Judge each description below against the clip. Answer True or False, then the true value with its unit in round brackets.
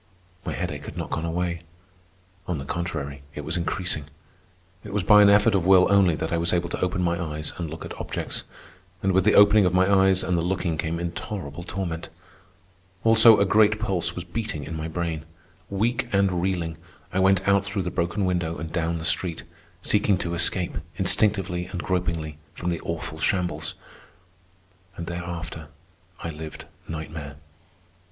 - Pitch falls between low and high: False (90 Hz)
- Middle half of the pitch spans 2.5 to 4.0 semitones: True (2.8 semitones)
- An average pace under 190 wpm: True (175 wpm)